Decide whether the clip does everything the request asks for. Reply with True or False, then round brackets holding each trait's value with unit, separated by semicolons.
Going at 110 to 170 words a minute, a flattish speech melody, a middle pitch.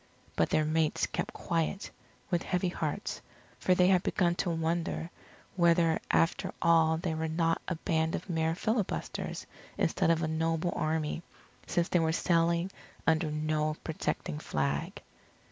True (145 wpm; 1.4 semitones; 165 Hz)